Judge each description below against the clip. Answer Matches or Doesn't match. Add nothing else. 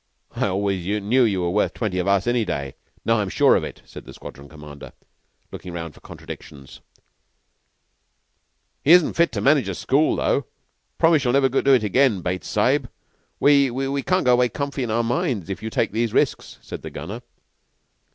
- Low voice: Matches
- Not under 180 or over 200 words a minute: Matches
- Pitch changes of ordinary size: Doesn't match